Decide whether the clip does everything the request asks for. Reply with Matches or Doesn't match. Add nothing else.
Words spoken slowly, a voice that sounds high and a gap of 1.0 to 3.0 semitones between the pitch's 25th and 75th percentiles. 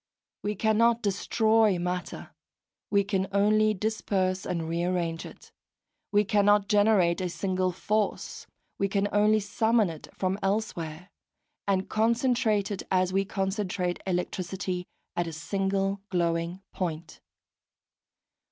Matches